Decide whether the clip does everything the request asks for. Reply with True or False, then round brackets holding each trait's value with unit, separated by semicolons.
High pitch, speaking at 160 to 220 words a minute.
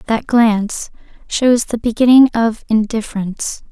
False (225 Hz; 115 wpm)